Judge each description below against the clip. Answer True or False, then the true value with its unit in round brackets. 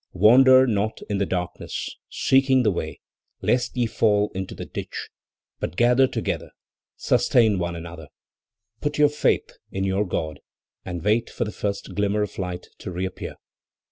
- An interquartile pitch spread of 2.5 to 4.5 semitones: False (4.9 semitones)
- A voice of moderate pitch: False (105 Hz)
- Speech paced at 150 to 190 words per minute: True (155 wpm)